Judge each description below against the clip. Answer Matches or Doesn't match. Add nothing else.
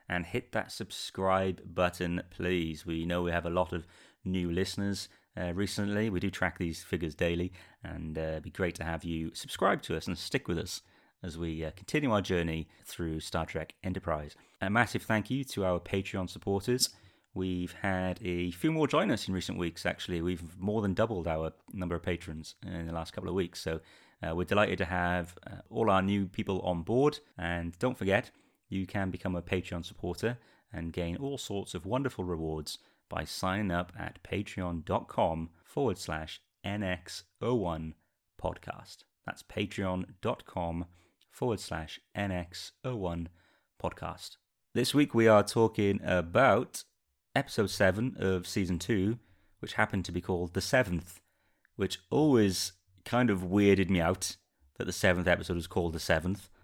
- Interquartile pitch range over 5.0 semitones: Doesn't match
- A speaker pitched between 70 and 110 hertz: Matches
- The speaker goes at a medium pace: Matches